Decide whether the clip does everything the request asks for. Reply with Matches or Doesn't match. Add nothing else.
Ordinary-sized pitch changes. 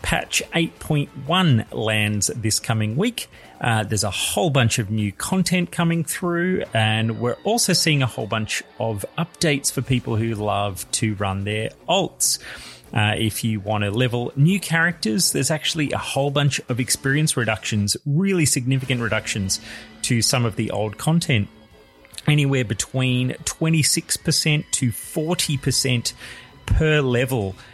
Doesn't match